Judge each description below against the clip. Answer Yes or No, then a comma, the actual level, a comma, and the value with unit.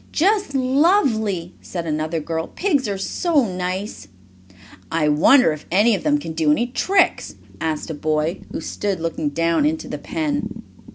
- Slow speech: No, average, 160 wpm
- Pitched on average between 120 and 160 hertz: No, high, 190 Hz